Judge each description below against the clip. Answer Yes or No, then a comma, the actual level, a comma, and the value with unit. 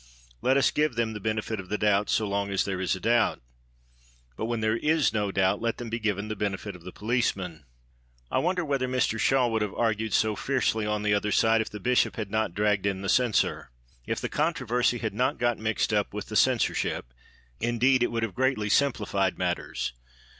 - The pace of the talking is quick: Yes, fast, 210 wpm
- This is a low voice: Yes, low, 110 Hz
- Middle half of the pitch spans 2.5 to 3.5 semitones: Yes, average, 2.9 semitones